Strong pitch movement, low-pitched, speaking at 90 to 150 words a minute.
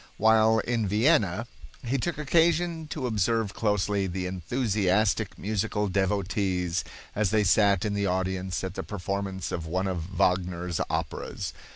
No: average, 3.1 semitones; low, 100 Hz; average, 140 wpm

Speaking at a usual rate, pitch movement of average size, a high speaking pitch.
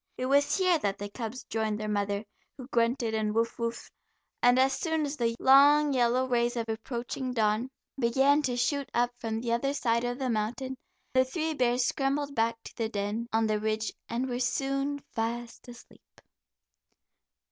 Yes: average, 180 wpm; average, 3.1 semitones; high, 240 Hz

